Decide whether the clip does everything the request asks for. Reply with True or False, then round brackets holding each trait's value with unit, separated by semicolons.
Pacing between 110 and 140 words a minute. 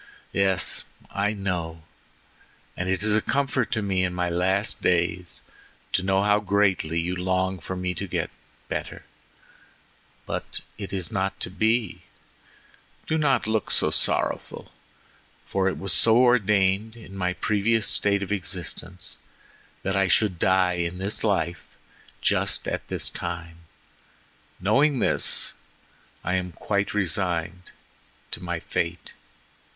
True (135 wpm)